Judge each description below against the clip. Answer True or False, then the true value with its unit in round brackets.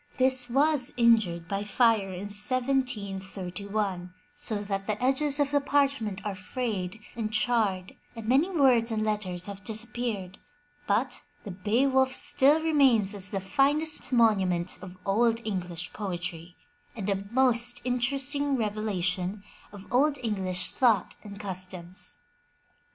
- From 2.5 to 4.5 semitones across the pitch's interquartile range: False (4.9 semitones)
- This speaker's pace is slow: True (130 wpm)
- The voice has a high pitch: True (215 Hz)